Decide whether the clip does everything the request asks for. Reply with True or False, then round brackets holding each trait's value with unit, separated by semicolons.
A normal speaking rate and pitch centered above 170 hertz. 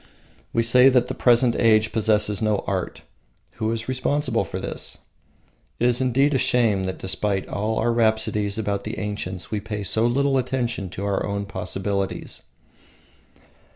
False (155 wpm; 110 Hz)